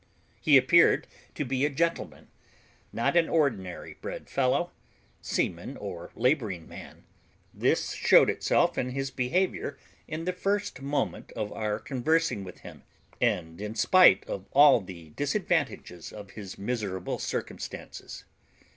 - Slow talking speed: Yes, slow, 130 wpm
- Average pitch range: No, wide, 7.6 semitones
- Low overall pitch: Yes, low, 130 Hz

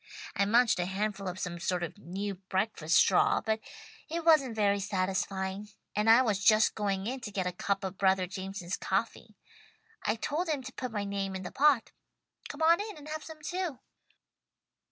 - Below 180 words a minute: No, average, 190 wpm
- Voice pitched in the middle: No, high, 205 Hz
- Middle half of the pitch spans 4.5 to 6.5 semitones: Yes, average, 5.2 semitones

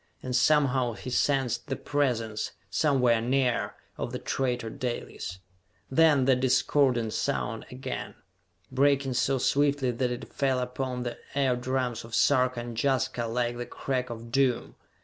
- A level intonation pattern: Yes, narrow, 2.1 semitones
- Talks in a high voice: No, low, 125 Hz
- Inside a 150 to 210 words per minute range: No, average, 140 wpm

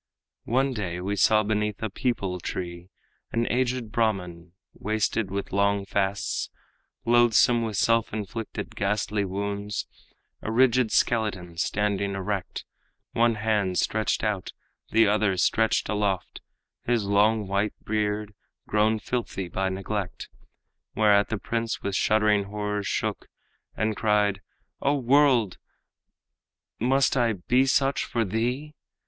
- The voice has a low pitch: Yes, low, 105 Hz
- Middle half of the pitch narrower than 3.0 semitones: Yes, narrow, 2.5 semitones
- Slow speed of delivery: Yes, slow, 120 wpm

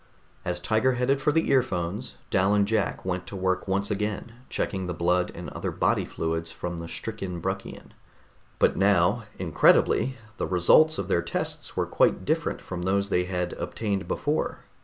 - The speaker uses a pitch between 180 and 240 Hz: No, very low, 95 Hz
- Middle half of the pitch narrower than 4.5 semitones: Yes, average, 3.6 semitones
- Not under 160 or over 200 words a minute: Yes, average, 170 wpm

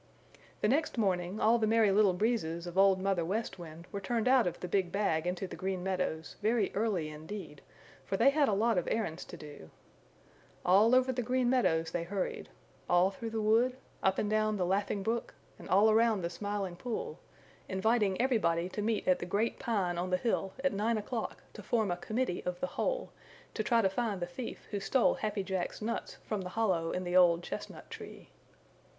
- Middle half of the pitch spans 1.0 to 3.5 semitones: No, average, 4.1 semitones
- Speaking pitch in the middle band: No, high, 200 Hz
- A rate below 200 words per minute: No, fast, 205 wpm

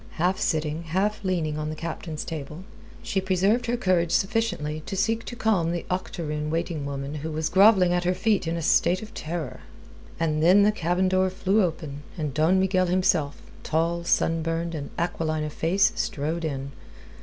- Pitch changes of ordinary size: Yes, average, 3.3 semitones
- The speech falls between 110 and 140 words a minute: No, average, 180 wpm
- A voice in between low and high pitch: Yes, medium, 170 Hz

